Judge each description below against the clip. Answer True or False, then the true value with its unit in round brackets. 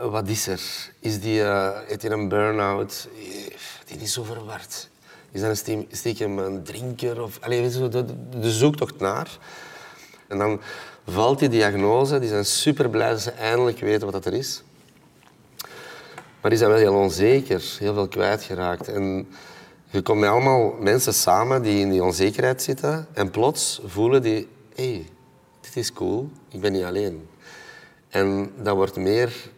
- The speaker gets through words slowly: False (165 wpm)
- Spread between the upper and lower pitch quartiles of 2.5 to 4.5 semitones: True (3.5 semitones)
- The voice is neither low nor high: False (110 Hz)